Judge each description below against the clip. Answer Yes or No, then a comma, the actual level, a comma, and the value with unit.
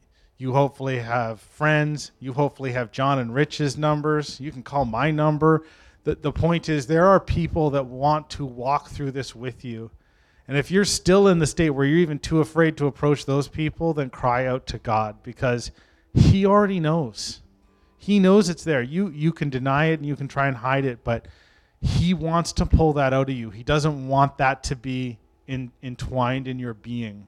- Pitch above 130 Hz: Yes, medium, 140 Hz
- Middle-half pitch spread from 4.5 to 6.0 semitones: No, average, 3.8 semitones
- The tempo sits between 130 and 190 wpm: No, average, 200 wpm